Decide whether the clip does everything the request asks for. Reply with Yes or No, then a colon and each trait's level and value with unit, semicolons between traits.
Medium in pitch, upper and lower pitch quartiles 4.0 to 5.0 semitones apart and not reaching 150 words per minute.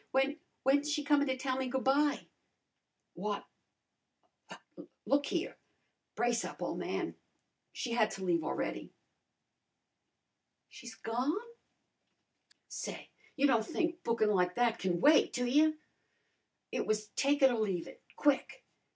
No: very high, 255 Hz; average, 4.7 semitones; average, 140 wpm